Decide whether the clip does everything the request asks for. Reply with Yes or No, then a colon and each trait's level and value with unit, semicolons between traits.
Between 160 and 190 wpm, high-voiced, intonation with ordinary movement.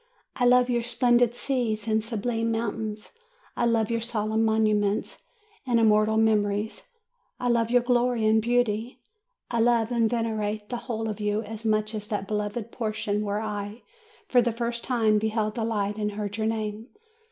No: average, 170 wpm; high, 220 Hz; narrow, 1.8 semitones